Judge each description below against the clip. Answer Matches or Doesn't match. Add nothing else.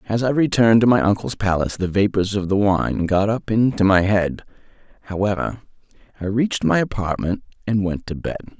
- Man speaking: Matches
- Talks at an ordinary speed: Matches